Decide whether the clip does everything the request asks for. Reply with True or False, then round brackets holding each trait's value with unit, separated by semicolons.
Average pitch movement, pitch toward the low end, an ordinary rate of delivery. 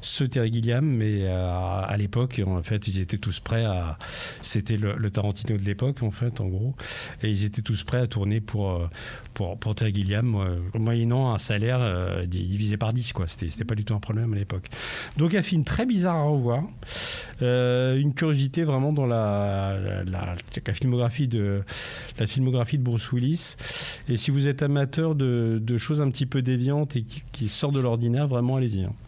True (4.2 semitones; 115 Hz; 205 wpm)